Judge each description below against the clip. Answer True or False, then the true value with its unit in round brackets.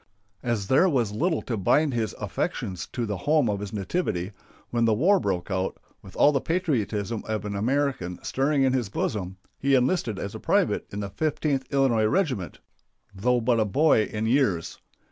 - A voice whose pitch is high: False (115 Hz)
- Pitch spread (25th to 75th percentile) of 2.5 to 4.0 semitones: False (5.4 semitones)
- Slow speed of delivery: False (185 wpm)